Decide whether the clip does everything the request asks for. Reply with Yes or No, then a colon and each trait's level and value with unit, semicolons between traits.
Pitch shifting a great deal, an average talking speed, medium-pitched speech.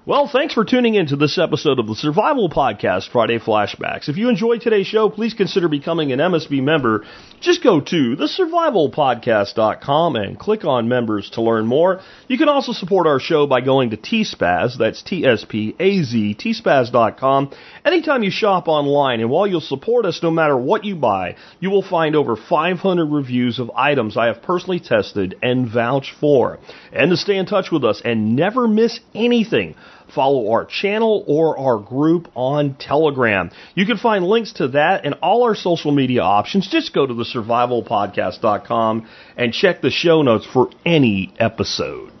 Yes: wide, 8.6 semitones; average, 180 wpm; medium, 155 Hz